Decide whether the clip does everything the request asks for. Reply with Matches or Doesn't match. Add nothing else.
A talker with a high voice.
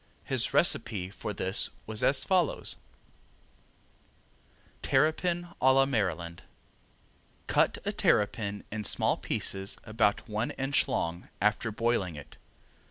Doesn't match